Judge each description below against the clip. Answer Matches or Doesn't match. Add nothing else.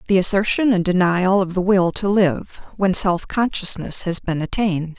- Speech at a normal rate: Matches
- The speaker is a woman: Matches